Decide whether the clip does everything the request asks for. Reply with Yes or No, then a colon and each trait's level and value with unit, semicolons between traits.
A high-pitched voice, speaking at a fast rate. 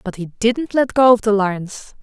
Yes: high, 215 Hz; fast, 235 wpm